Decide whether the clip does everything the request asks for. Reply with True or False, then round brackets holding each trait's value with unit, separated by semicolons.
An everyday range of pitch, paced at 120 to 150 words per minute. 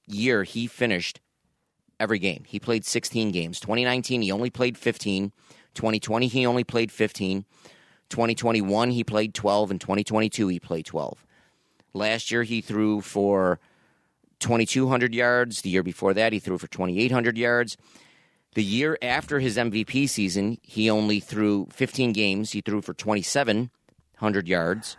True (3.1 semitones; 145 wpm)